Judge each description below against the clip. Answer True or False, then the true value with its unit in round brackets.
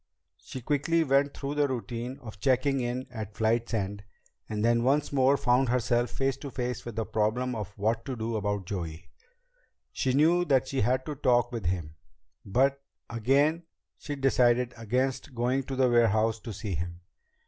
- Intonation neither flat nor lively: True (3.5 semitones)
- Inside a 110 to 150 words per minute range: False (175 wpm)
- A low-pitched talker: True (120 Hz)